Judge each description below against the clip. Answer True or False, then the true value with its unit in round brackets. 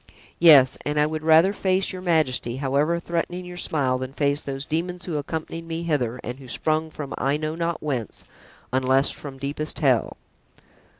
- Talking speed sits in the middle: True (175 wpm)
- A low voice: False (150 Hz)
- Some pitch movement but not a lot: True (3.7 semitones)